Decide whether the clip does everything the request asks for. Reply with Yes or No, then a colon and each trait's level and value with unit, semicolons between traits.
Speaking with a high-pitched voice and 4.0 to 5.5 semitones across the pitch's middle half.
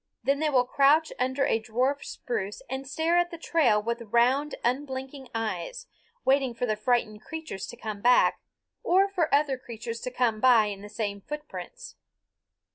Yes: very high, 255 Hz; average, 4.6 semitones